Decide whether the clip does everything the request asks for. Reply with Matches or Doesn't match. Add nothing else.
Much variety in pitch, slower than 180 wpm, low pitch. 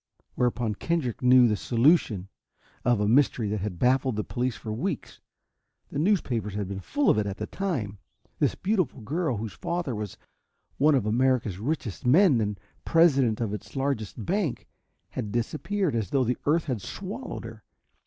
Matches